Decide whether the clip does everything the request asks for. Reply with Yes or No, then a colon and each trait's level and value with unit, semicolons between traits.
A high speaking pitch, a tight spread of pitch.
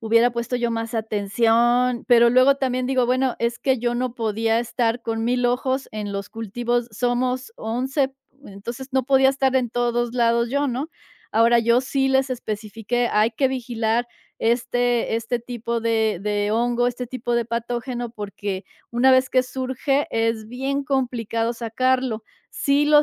Yes: high, 240 Hz; narrow, 2.1 semitones